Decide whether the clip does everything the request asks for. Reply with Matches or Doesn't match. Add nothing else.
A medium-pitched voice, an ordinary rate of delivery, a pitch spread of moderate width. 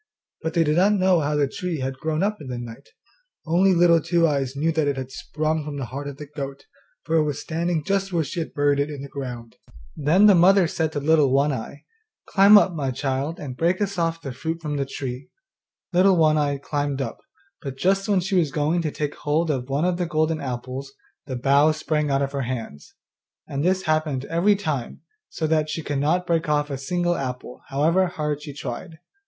Doesn't match